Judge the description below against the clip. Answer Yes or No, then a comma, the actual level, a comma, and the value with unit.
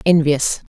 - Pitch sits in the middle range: Yes, medium, 155 Hz